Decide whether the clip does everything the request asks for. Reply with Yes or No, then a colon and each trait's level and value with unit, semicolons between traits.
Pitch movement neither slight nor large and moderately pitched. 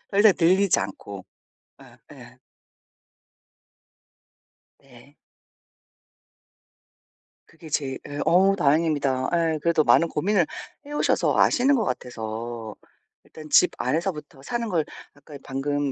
Yes: average, 4.8 semitones; medium, 155 Hz